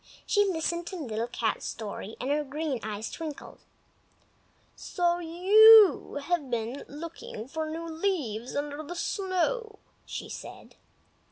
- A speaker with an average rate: No, slow, 125 wpm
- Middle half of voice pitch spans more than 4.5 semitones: Yes, wide, 5.4 semitones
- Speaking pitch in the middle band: No, very high, 320 Hz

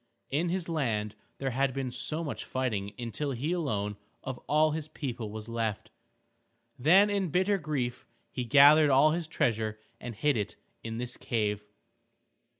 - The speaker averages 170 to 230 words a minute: No, average, 150 wpm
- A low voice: Yes, low, 130 Hz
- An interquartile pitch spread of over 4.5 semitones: Yes, wide, 5.4 semitones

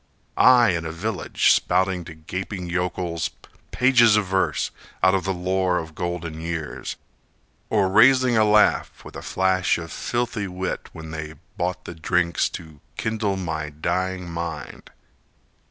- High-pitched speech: No, very low, 90 Hz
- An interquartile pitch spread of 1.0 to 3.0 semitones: Yes, narrow, 2.6 semitones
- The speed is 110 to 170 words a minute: Yes, average, 145 wpm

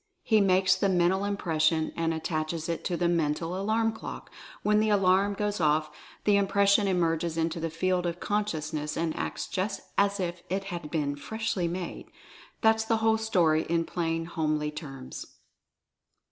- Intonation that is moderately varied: Yes, average, 3.7 semitones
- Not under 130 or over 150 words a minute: No, average, 170 wpm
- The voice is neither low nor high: Yes, medium, 175 Hz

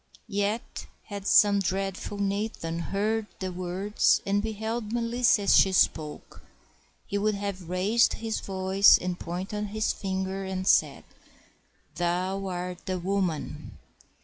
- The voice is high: Yes, high, 195 Hz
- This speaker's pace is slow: Yes, slow, 125 wpm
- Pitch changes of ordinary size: No, narrow, 2.2 semitones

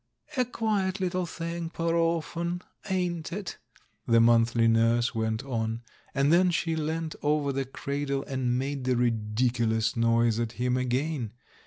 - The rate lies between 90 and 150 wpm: Yes, average, 145 wpm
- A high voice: No, low, 135 Hz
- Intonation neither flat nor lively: No, wide, 6.2 semitones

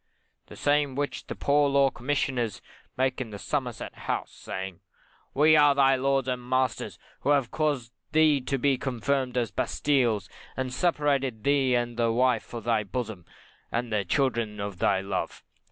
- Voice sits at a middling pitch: No, low, 130 Hz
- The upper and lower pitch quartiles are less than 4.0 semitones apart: Yes, average, 3.4 semitones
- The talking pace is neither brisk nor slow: Yes, average, 165 wpm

